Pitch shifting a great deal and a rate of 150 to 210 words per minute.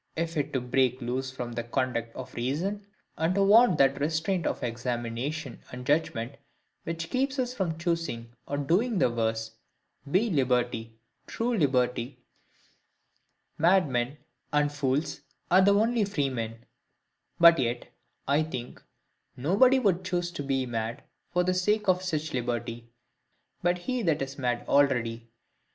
No: wide, 6.6 semitones; average, 140 wpm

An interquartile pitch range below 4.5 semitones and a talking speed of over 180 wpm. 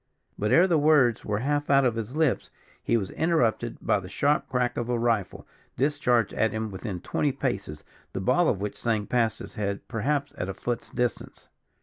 No: average, 4.9 semitones; average, 200 wpm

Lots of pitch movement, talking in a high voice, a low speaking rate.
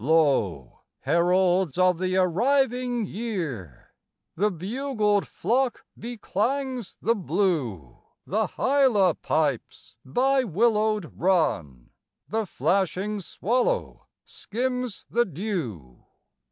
Yes: wide, 6.4 semitones; high, 195 Hz; slow, 85 wpm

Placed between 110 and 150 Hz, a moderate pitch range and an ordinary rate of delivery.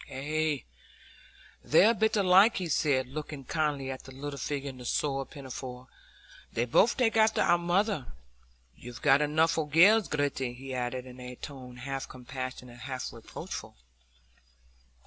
Yes: medium, 140 Hz; average, 3.8 semitones; average, 150 wpm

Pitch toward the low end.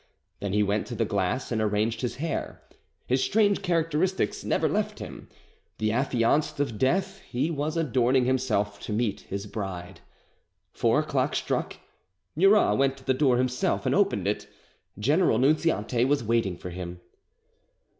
Yes: low, 125 Hz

